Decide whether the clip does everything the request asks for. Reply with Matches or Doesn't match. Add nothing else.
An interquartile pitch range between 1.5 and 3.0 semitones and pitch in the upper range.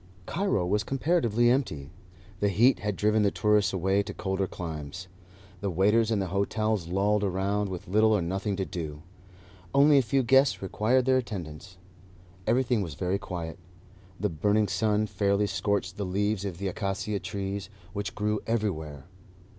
Doesn't match